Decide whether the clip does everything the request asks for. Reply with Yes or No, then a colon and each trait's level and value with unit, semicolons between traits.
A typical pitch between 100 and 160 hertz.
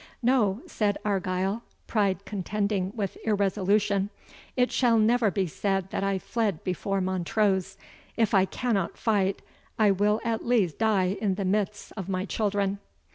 No: high, 200 Hz